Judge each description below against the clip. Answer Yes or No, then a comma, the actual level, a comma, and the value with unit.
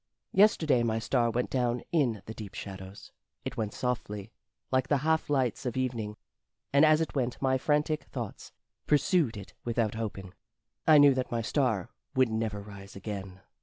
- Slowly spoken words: No, average, 165 wpm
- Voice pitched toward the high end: No, low, 120 Hz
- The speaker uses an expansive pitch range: No, average, 4.6 semitones